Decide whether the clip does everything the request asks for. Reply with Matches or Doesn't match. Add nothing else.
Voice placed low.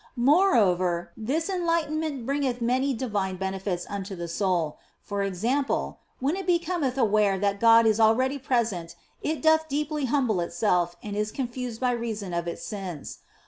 Doesn't match